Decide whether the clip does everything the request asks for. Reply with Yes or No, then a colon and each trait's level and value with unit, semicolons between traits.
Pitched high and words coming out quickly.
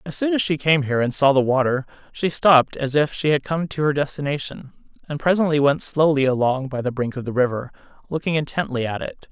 No: medium, 140 Hz; fast, 225 wpm